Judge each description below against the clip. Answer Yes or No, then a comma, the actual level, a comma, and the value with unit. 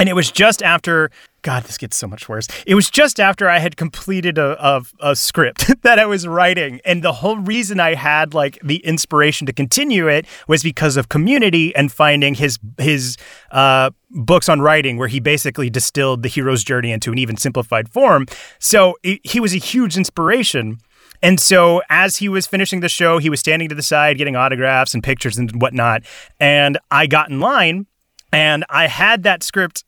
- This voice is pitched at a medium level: Yes, medium, 150 Hz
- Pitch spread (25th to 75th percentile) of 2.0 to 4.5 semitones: No, average, 5.1 semitones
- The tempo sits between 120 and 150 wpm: No, average, 200 wpm